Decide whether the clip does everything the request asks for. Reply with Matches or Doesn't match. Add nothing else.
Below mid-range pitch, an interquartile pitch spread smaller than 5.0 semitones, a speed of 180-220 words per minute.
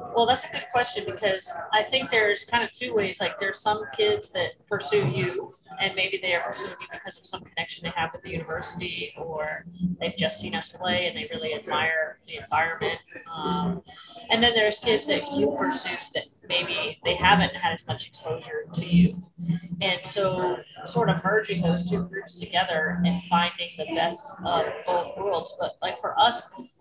Doesn't match